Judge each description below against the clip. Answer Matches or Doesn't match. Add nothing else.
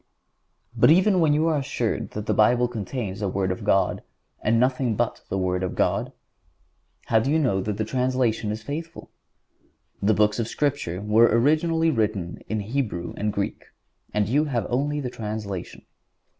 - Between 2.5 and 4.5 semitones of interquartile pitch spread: Doesn't match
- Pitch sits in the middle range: Doesn't match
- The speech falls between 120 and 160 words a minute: Doesn't match